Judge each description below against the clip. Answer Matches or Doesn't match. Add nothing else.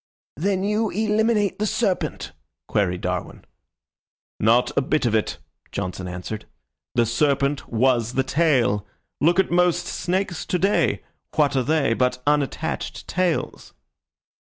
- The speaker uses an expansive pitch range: Matches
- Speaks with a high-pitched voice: Doesn't match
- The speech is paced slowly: Matches